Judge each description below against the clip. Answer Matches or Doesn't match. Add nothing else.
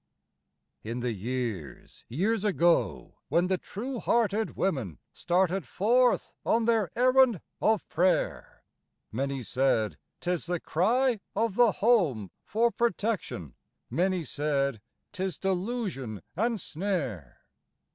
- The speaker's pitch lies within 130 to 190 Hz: Matches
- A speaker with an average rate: Doesn't match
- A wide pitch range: Matches